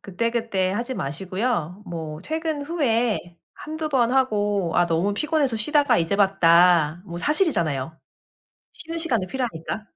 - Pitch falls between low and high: No, high, 210 Hz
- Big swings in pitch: Yes, wide, 7.4 semitones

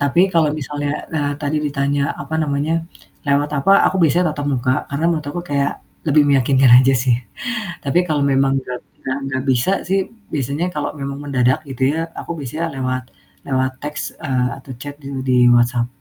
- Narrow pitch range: Yes, narrow, 2.2 semitones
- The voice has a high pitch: No, medium, 140 Hz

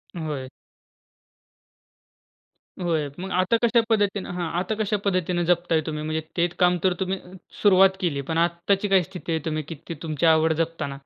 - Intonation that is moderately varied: Yes, average, 3.1 semitones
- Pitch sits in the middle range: Yes, medium, 175 Hz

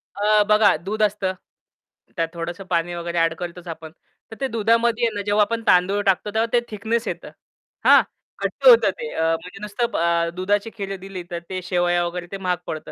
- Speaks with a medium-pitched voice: No, high, 195 Hz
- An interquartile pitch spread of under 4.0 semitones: Yes, average, 3.5 semitones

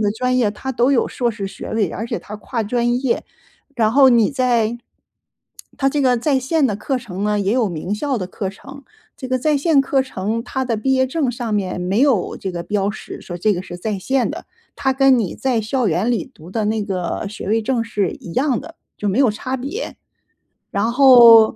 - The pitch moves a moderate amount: Yes, average, 4.2 semitones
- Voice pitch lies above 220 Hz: Yes, high, 235 Hz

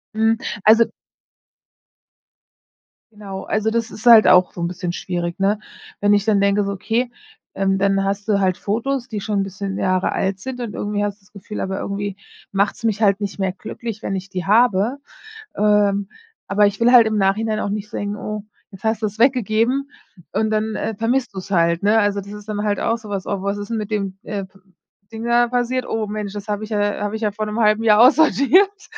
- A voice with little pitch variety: Yes, narrow, 2.1 semitones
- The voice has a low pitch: No, high, 210 Hz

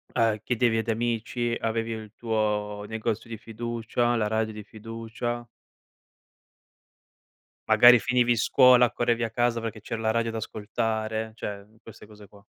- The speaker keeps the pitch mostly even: Yes, narrow, 1.5 semitones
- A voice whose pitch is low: Yes, low, 115 Hz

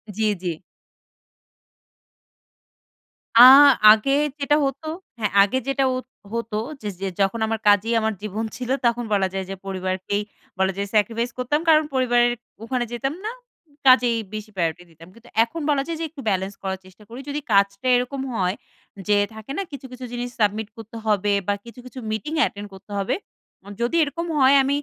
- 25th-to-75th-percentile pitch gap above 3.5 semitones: Yes, average, 4.1 semitones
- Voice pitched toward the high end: Yes, high, 230 Hz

